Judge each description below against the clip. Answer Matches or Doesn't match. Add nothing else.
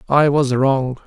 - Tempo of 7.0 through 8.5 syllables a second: Doesn't match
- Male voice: Matches